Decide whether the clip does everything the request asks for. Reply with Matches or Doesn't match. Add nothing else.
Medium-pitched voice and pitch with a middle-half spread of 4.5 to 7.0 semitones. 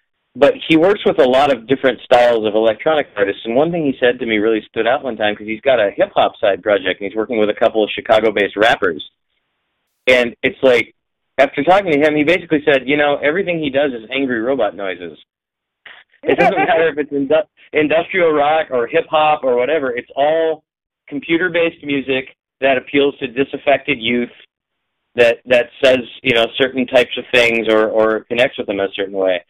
Doesn't match